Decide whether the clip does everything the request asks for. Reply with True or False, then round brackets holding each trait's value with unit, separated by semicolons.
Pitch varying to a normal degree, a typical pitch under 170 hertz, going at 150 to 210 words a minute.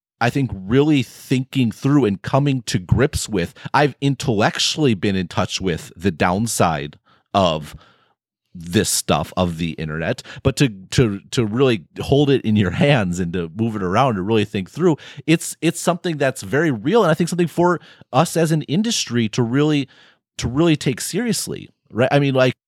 False (5.9 semitones; 135 Hz; 180 wpm)